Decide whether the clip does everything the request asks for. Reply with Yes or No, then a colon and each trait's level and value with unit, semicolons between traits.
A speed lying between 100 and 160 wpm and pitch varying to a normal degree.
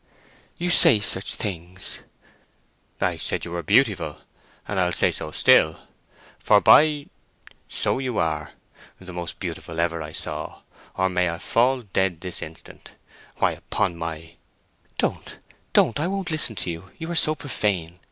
No: average, 150 wpm; wide, 6.8 semitones